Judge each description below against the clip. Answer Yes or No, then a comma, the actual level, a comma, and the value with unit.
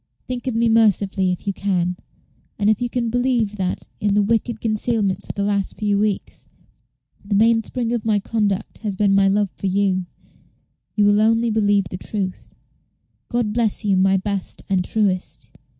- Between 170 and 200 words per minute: Yes, average, 175 wpm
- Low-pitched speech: No, high, 205 Hz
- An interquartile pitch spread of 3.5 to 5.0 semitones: No, narrow, 2.4 semitones